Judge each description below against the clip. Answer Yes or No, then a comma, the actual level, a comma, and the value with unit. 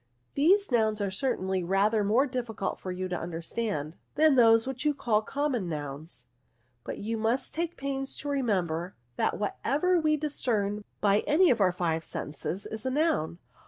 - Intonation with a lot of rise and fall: Yes, wide, 6.7 semitones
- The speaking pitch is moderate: No, high, 220 Hz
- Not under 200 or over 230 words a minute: No, average, 170 wpm